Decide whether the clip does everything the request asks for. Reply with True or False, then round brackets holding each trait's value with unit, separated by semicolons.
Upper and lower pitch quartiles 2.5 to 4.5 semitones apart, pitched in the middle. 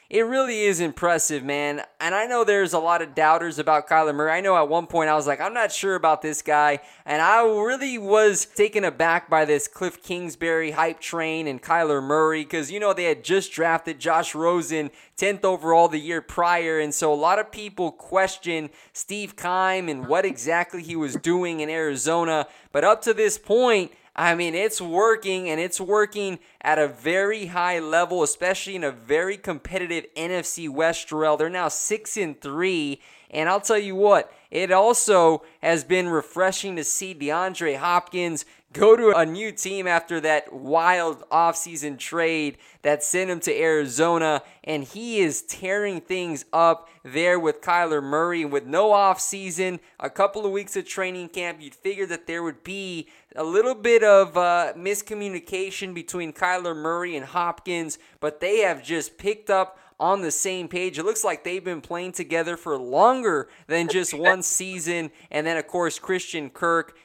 True (3.2 semitones; 170 Hz)